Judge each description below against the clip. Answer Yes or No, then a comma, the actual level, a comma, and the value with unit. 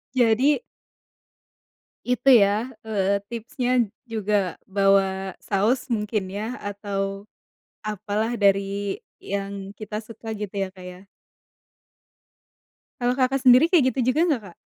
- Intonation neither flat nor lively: Yes, average, 3.6 semitones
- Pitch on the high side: Yes, high, 210 Hz